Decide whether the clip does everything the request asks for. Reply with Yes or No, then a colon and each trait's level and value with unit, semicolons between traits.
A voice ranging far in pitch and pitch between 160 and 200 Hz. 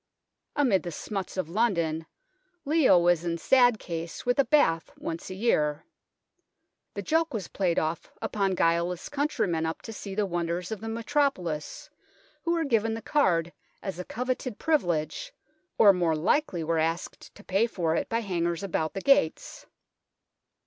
Yes: wide, 6.2 semitones; high, 190 Hz